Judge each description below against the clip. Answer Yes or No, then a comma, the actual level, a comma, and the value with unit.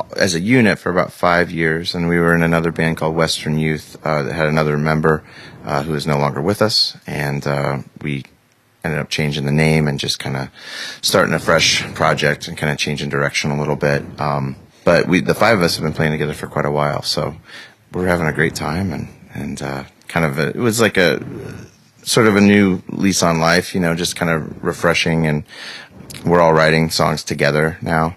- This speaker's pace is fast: Yes, fast, 220 wpm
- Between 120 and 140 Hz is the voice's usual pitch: No, very low, 80 Hz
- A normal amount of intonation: No, narrow, 2.3 semitones